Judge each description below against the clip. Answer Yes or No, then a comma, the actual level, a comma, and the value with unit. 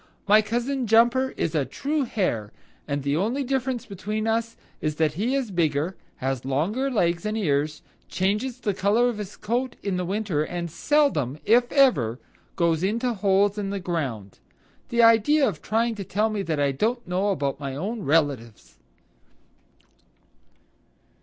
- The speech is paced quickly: No, average, 155 wpm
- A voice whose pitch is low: No, high, 200 Hz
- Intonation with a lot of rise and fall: Yes, wide, 7.2 semitones